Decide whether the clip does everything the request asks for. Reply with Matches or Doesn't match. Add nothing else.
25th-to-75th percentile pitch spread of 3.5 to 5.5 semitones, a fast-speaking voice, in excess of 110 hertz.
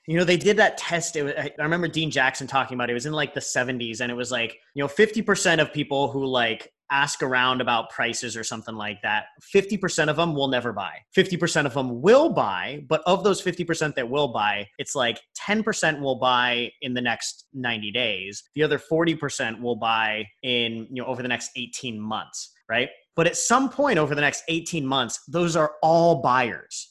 Matches